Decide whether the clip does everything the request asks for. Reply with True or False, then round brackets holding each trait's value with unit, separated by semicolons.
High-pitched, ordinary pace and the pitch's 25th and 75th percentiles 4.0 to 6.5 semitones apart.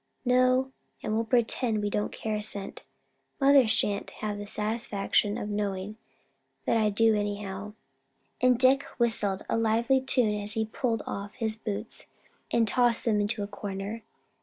False (215 Hz; 160 wpm; 2.4 semitones)